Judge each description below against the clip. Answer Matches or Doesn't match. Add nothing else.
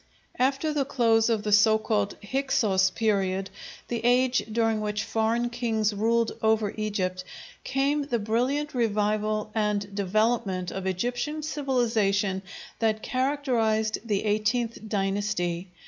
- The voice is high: Matches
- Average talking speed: Doesn't match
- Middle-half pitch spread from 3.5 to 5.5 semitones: Doesn't match